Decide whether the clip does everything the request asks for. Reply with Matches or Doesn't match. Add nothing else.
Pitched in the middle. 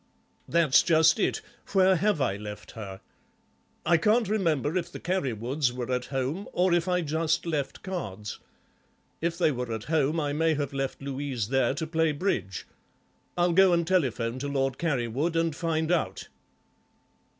Matches